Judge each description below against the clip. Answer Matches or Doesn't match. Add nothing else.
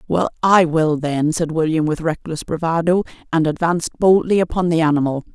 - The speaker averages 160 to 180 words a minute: Matches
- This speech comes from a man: Doesn't match